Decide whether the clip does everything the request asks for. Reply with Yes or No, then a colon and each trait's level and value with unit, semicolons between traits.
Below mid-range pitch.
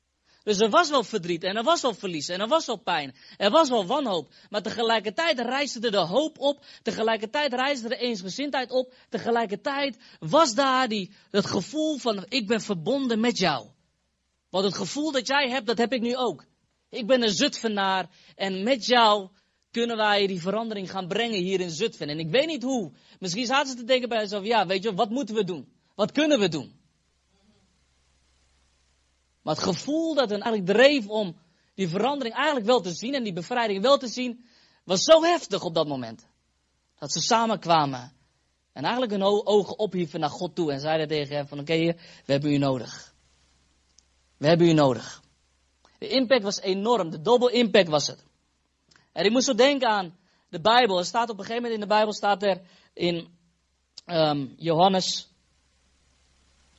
No: high, 205 Hz